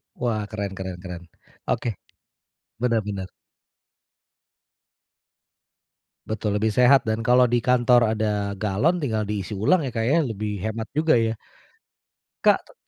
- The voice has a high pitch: No, low, 110 Hz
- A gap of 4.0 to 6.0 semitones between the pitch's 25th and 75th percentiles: No, average, 2.9 semitones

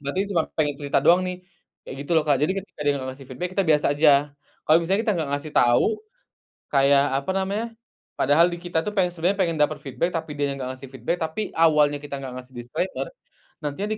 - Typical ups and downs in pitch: Yes, average, 4.0 semitones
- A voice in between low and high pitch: Yes, medium, 150 Hz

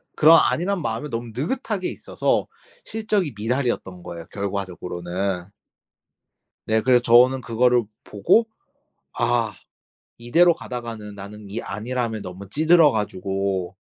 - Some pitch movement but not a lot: No, wide, 6.7 semitones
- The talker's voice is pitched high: No, low, 115 Hz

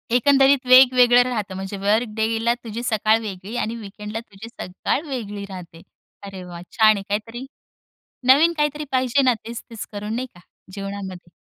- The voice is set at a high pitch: Yes, high, 220 Hz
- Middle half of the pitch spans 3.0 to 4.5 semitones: Yes, average, 3.9 semitones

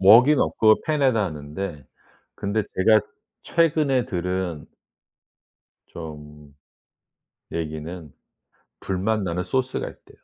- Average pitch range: No, wide, 6.2 semitones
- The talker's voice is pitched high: No, very low, 95 Hz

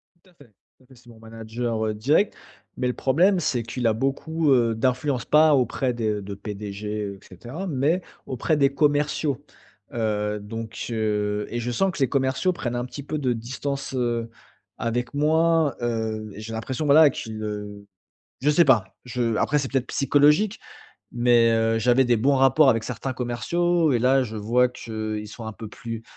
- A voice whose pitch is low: Yes, low, 120 Hz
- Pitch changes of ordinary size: Yes, average, 4.1 semitones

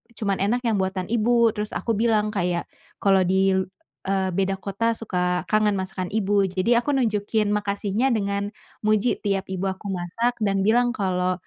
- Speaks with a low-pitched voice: No, high, 200 Hz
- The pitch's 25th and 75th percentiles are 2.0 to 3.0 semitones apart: Yes, narrow, 2.6 semitones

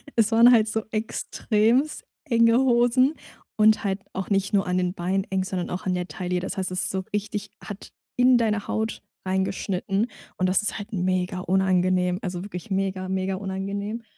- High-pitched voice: Yes, high, 195 Hz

